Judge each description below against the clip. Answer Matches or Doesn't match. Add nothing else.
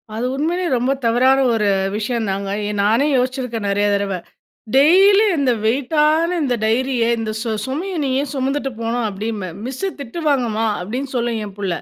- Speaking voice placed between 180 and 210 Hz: Doesn't match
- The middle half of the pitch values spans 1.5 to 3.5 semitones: Doesn't match